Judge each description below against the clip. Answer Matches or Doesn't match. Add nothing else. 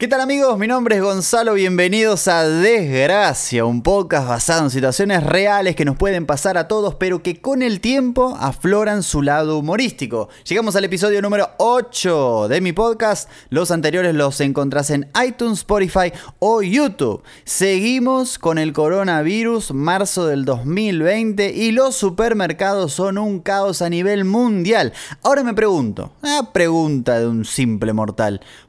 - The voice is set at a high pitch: Matches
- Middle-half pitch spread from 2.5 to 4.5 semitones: Doesn't match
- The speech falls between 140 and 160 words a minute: Matches